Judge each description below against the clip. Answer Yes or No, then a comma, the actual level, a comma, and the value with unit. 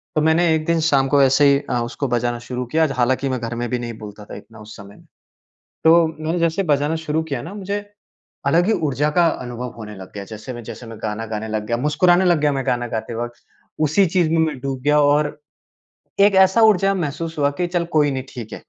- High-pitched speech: No, medium, 140 Hz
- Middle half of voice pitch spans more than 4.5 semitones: Yes, average, 5.2 semitones